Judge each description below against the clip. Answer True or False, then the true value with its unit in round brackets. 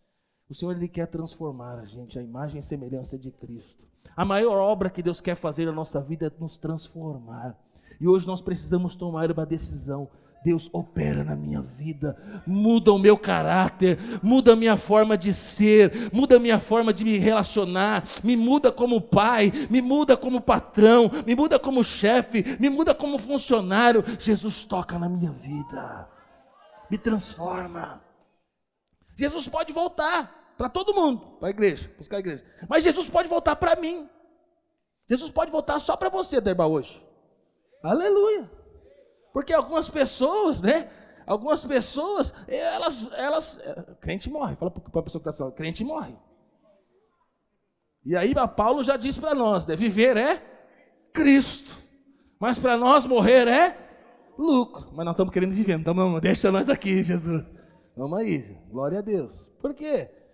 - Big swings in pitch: True (8.3 semitones)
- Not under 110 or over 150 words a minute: False (160 wpm)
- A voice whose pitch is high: True (215 Hz)